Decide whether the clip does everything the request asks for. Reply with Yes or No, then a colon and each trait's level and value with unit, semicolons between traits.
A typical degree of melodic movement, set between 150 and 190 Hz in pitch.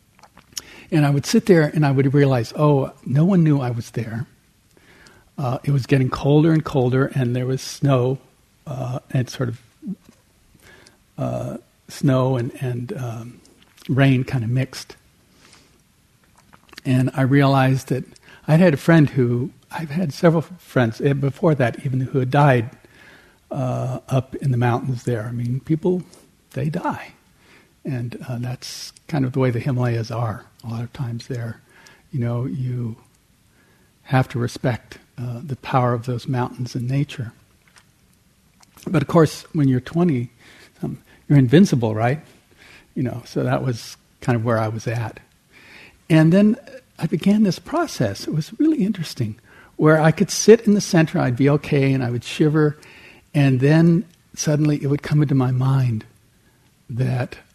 No: average, 3.9 semitones; low, 135 Hz